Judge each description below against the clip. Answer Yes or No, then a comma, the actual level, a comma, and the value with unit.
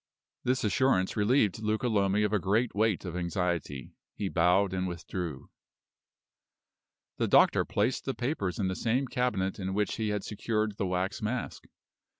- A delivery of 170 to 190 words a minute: No, average, 155 wpm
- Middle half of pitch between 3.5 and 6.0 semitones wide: No, average, 3.1 semitones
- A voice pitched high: No, low, 100 Hz